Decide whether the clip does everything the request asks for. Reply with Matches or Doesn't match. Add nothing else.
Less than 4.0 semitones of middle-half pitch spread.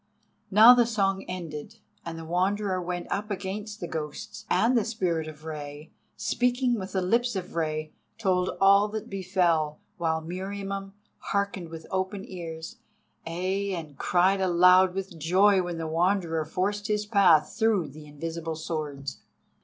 Matches